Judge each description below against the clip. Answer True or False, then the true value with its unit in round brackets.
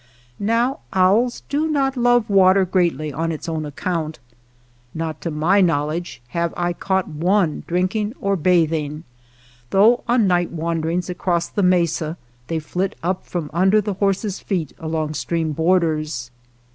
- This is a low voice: False (175 Hz)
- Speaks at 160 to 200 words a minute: False (145 wpm)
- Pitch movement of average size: True (3.6 semitones)